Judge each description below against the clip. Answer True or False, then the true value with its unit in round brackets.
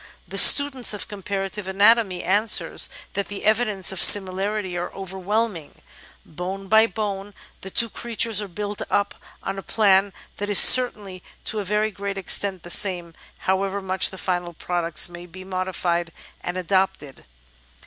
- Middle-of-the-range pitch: False (195 Hz)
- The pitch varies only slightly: True (2.1 semitones)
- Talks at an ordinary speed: True (150 wpm)